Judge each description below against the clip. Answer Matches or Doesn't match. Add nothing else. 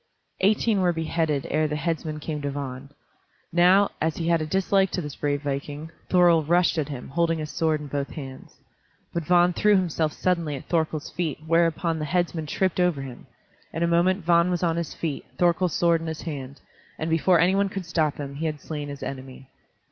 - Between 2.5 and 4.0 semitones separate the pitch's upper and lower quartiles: Matches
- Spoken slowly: Doesn't match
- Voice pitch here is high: Doesn't match